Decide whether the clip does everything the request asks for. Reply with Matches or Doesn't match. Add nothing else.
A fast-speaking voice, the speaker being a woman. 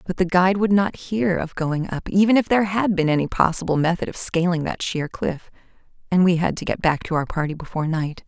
Matches